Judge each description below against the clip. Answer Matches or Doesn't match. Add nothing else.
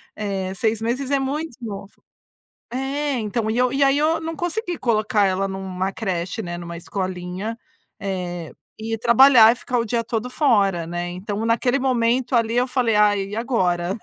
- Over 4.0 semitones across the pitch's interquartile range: Matches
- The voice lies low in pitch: Doesn't match